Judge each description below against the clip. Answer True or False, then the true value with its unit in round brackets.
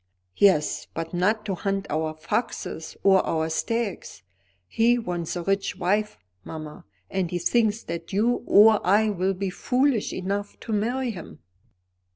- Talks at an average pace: True (150 wpm)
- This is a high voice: True (195 Hz)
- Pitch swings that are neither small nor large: True (3.9 semitones)